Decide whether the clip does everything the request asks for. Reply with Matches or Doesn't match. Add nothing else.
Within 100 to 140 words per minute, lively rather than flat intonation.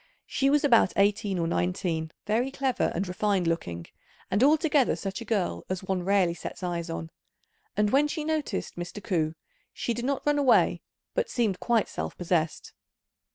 Doesn't match